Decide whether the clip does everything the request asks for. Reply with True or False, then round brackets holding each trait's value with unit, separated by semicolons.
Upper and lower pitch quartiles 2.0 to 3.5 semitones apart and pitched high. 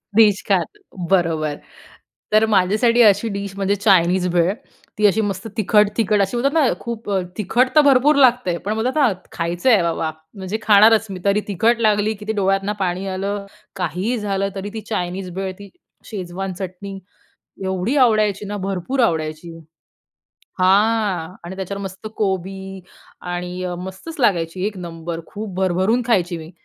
True (2.9 semitones; 195 Hz)